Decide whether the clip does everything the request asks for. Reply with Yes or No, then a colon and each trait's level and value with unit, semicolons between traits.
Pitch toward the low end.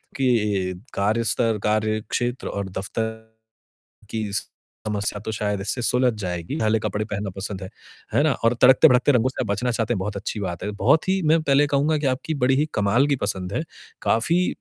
Yes: low, 110 Hz